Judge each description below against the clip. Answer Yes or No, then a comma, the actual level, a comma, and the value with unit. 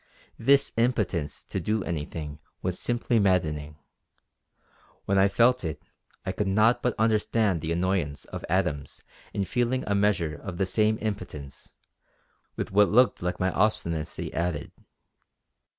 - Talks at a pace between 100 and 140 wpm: Yes, slow, 135 wpm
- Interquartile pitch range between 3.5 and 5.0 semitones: Yes, average, 4.6 semitones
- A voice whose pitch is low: Yes, very low, 95 Hz